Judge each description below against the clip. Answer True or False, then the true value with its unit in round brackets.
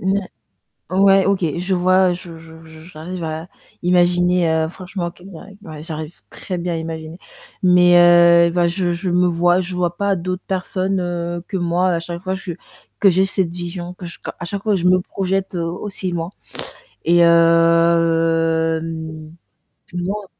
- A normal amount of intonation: False (1.8 semitones)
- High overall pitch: False (175 Hz)